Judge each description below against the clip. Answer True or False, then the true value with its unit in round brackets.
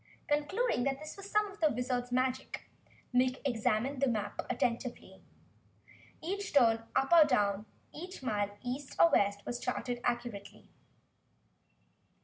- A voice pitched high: True (255 Hz)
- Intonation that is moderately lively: True (3.9 semitones)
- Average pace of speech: False (130 wpm)